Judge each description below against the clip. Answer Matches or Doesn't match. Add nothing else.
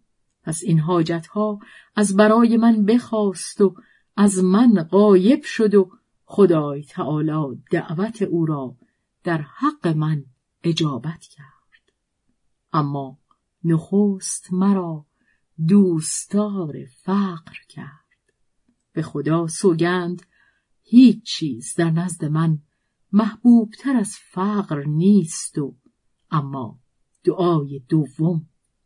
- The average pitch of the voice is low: Doesn't match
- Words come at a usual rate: Doesn't match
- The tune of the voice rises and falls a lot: Doesn't match